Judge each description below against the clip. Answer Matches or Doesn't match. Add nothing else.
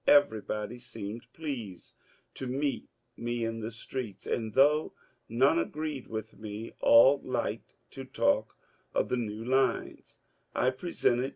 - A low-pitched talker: Matches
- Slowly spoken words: Matches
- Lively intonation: Doesn't match